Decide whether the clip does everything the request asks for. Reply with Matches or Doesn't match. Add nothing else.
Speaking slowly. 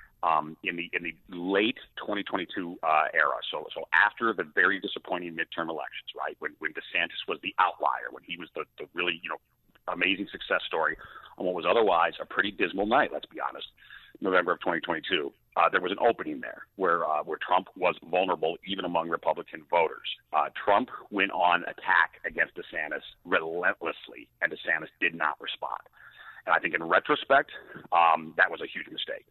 Doesn't match